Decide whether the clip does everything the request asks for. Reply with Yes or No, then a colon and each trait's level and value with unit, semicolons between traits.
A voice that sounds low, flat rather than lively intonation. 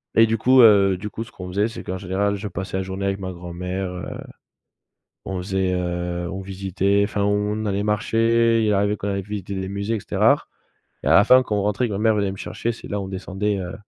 Yes: low, 100 Hz; narrow, 1.8 semitones